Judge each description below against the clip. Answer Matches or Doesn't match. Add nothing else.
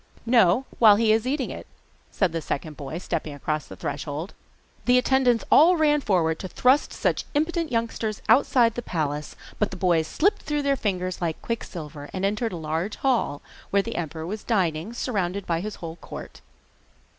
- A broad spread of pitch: Matches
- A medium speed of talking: Matches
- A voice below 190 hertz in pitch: Doesn't match